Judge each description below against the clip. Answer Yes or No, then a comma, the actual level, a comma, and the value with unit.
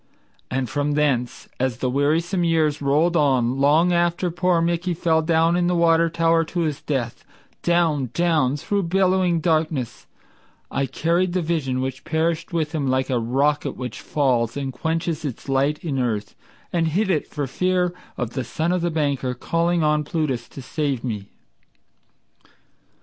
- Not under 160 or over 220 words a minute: Yes, average, 165 wpm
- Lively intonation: No, average, 4.2 semitones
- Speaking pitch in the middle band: Yes, medium, 155 Hz